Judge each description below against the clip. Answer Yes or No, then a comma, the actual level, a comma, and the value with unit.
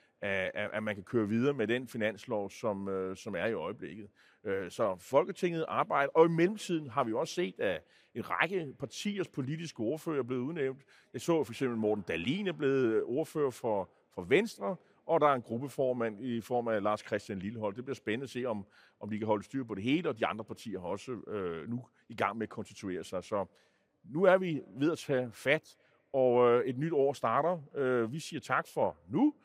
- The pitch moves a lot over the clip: Yes, wide, 6.4 semitones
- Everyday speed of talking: Yes, average, 200 wpm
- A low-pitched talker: Yes, low, 130 Hz